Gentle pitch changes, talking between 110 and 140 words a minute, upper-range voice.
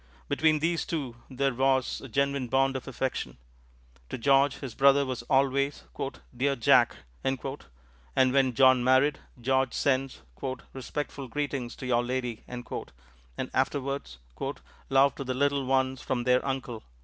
No: narrow, 1.9 semitones; slow, 135 wpm; low, 130 Hz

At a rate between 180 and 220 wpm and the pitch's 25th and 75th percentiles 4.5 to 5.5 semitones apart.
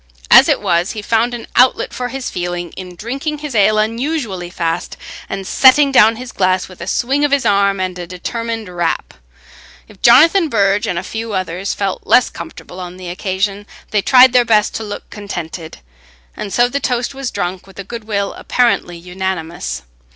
Yes: average, 185 wpm; average, 4.9 semitones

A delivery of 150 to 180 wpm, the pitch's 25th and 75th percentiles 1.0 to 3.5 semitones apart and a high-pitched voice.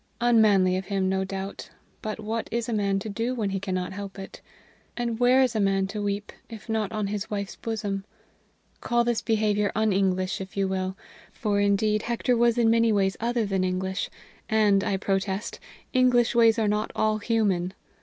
No: average, 190 wpm; average, 2.7 semitones; high, 210 Hz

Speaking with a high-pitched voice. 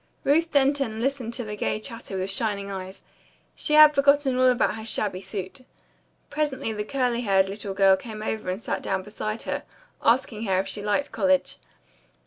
Yes: high, 220 Hz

